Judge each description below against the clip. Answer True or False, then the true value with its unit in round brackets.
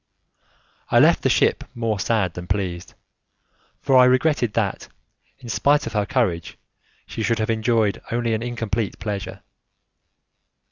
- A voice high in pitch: False (110 Hz)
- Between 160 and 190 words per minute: False (140 wpm)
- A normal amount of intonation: True (3.1 semitones)